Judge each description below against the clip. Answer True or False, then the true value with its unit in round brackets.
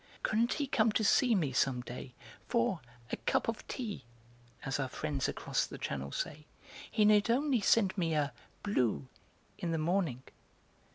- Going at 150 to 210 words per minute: True (160 wpm)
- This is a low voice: False (180 Hz)